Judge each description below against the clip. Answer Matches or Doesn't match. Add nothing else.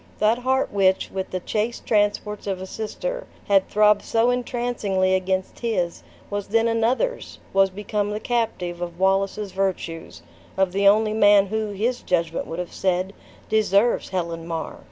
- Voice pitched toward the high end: Matches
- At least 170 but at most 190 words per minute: Doesn't match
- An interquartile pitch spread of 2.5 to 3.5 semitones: Matches